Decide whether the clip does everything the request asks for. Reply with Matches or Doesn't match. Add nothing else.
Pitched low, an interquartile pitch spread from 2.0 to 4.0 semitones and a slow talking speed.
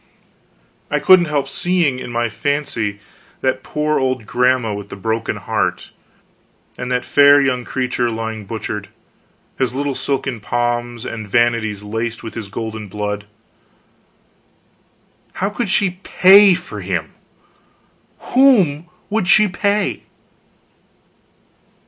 Doesn't match